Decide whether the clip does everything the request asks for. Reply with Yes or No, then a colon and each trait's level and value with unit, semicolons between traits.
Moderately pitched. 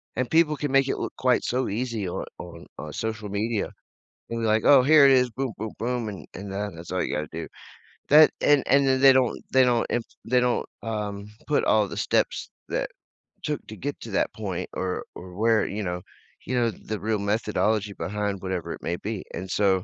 No: low, 110 Hz